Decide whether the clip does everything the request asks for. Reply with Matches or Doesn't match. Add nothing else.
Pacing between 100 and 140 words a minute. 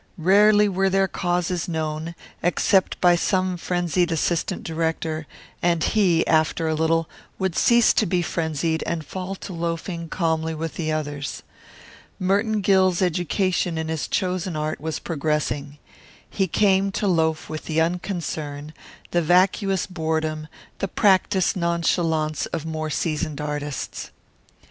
Matches